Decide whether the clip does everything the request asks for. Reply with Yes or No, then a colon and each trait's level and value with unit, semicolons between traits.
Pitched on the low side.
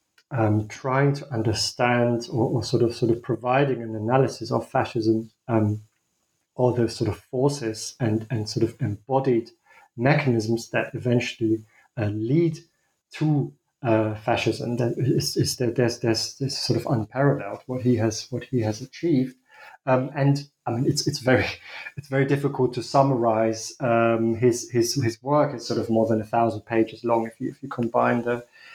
Yes: low, 120 Hz